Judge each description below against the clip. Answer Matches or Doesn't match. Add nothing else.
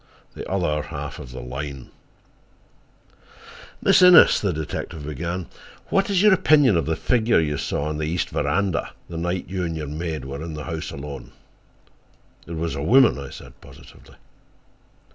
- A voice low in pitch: Matches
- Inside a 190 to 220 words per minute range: Doesn't match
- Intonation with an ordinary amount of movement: Matches